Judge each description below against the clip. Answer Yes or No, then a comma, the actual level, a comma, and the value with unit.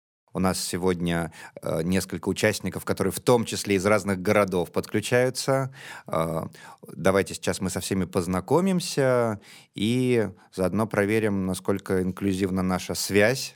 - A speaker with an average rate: Yes, average, 125 wpm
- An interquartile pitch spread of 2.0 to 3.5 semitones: Yes, average, 2.8 semitones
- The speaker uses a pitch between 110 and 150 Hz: No, very low, 95 Hz